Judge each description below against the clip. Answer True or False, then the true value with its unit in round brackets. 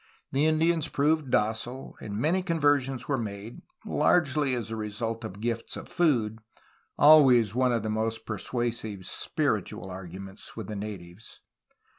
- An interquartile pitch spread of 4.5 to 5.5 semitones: True (4.9 semitones)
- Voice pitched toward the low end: True (115 Hz)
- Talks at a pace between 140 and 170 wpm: True (145 wpm)